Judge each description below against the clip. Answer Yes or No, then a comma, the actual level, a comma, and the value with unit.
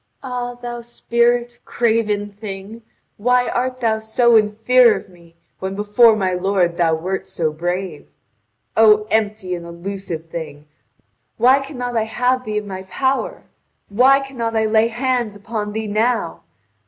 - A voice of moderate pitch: No, high, 220 Hz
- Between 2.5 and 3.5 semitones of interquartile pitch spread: No, average, 4.0 semitones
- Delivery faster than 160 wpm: No, average, 150 wpm